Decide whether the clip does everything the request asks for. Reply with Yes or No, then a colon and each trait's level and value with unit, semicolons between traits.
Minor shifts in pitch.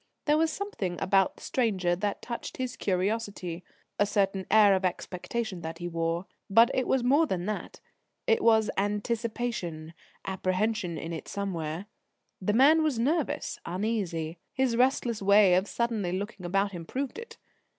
No: average, 4.6 semitones